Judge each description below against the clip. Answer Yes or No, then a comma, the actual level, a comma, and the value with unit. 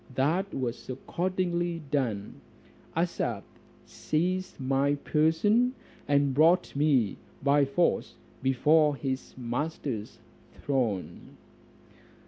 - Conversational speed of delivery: No, slow, 85 wpm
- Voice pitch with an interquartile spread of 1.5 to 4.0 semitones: No, average, 4.5 semitones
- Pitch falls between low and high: Yes, medium, 145 Hz